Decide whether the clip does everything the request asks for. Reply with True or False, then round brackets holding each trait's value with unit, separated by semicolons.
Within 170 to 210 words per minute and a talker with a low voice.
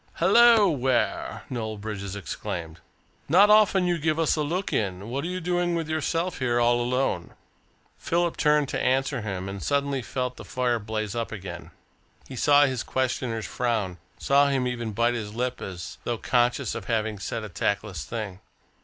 True (175 wpm; 125 Hz)